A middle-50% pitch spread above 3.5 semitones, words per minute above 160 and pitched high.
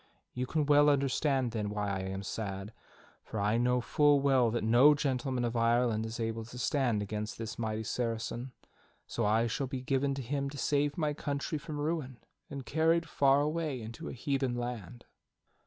No: average, 4.0 semitones; average, 185 wpm; low, 125 Hz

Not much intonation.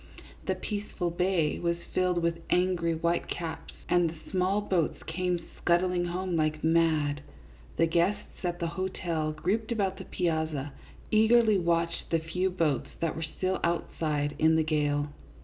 Yes: narrow, 2.3 semitones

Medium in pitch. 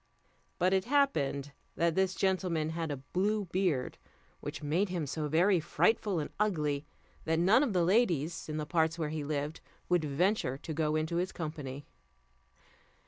Yes: medium, 165 Hz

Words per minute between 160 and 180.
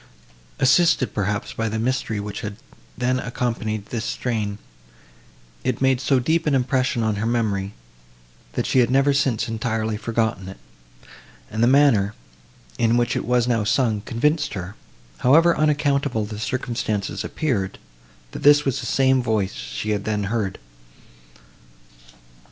No: average, 145 wpm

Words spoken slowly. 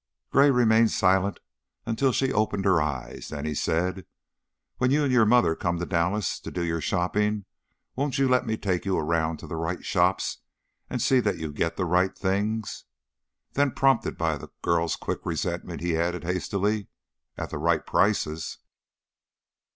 No: average, 175 wpm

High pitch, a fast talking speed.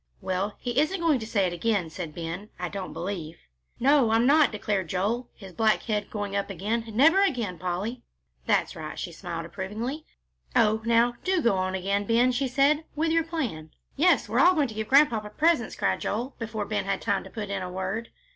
Yes: high, 220 Hz; fast, 210 wpm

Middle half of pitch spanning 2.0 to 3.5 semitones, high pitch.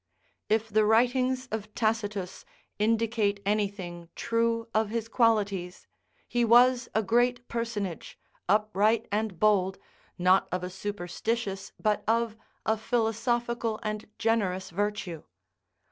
Yes: narrow, 2.4 semitones; high, 215 Hz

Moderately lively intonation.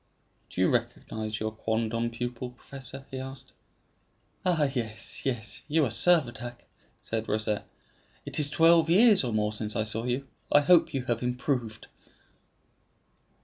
Yes: average, 4.1 semitones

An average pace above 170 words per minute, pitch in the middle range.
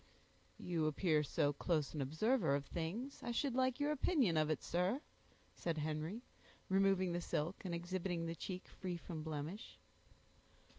No: average, 155 wpm; medium, 175 Hz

